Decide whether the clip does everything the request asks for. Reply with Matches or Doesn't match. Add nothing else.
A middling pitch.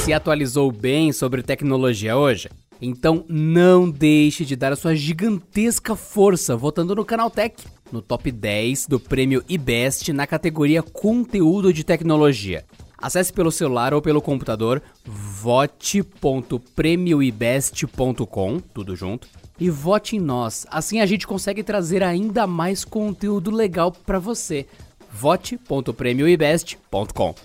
Matches